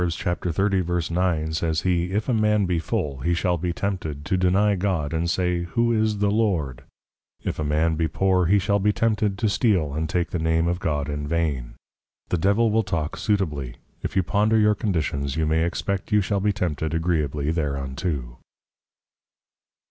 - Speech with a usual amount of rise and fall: Yes, average, 4.3 semitones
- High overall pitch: No, very low, 85 Hz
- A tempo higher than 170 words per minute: Yes, average, 180 wpm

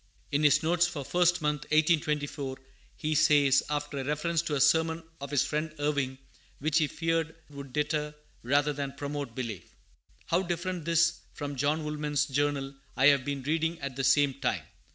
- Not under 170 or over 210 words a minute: Yes, average, 175 wpm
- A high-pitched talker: No, medium, 150 Hz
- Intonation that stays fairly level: Yes, narrow, 2.2 semitones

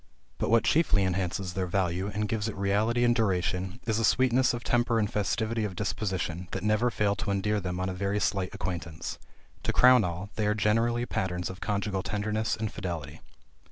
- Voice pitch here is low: Yes, low, 100 Hz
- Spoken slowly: No, average, 190 wpm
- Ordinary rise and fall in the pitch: Yes, average, 3.0 semitones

